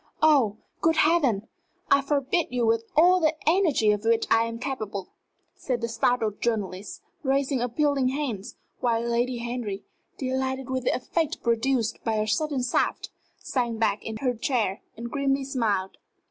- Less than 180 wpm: Yes, average, 155 wpm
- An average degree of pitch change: Yes, average, 3.5 semitones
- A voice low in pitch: No, high, 245 Hz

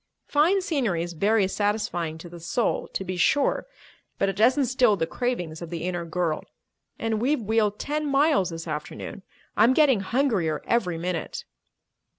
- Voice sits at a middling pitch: No, high, 205 Hz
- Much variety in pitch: Yes, wide, 6.6 semitones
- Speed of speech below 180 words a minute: Yes, average, 160 wpm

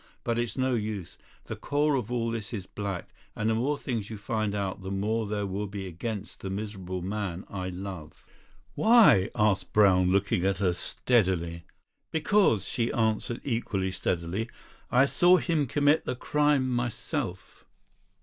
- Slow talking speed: No, average, 160 wpm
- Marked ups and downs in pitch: No, average, 4.2 semitones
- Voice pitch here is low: Yes, low, 105 Hz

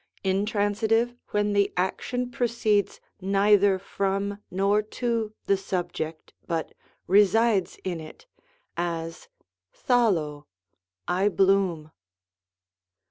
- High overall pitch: Yes, high, 200 Hz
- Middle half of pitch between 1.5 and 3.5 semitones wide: Yes, average, 2.9 semitones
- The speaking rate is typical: No, slow, 90 wpm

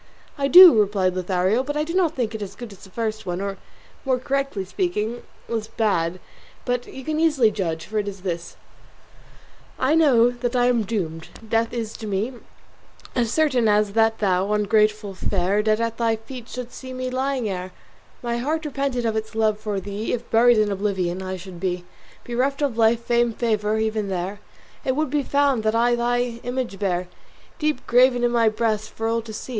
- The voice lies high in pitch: Yes, high, 225 Hz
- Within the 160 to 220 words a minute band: Yes, average, 200 wpm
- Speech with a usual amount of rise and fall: Yes, average, 3.5 semitones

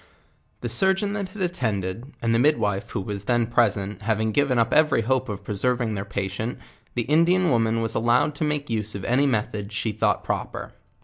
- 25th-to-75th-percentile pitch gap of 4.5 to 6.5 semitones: Yes, average, 5.2 semitones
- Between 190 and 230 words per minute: Yes, average, 195 wpm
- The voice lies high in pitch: No, low, 115 Hz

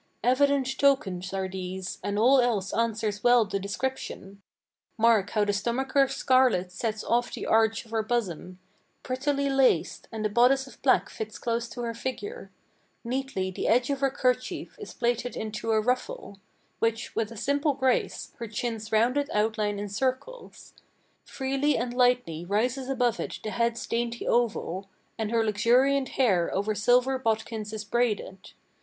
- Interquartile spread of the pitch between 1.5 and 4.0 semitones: Yes, average, 3.6 semitones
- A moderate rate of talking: Yes, average, 155 wpm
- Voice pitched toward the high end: Yes, high, 235 Hz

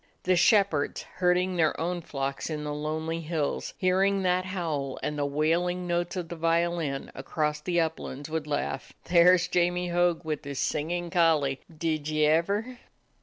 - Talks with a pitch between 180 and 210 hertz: No, medium, 165 Hz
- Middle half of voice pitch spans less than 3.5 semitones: Yes, average, 2.8 semitones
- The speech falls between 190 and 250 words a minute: No, average, 165 wpm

